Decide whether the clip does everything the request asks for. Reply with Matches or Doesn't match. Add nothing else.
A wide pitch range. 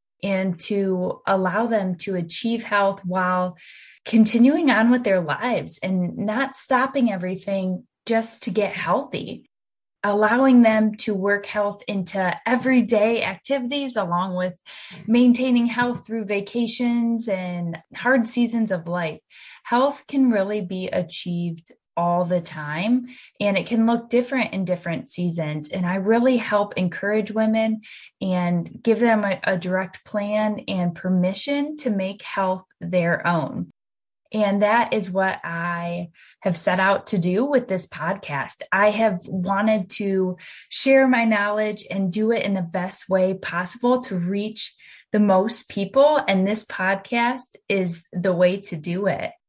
Doesn't match